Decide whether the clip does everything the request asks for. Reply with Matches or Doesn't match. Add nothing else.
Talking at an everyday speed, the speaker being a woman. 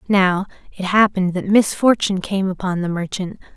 Matches